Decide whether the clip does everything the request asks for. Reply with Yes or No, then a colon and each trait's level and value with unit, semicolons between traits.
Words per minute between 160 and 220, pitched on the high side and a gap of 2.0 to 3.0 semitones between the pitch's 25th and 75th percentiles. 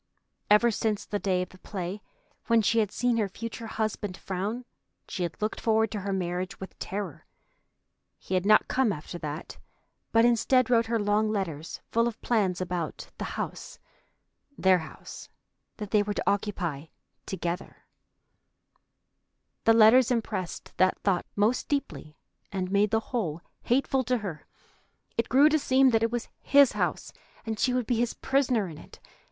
No: average, 165 wpm; high, 210 Hz; average, 3.8 semitones